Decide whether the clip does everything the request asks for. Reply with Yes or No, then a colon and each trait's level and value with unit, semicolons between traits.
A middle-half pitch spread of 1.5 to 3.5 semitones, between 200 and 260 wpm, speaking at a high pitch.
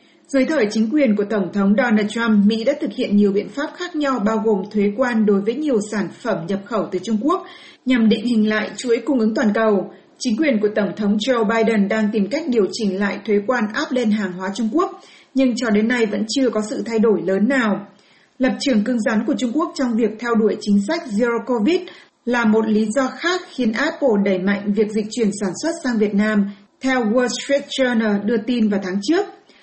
No: average, 3.9 semitones; average, 235 wpm; high, 225 Hz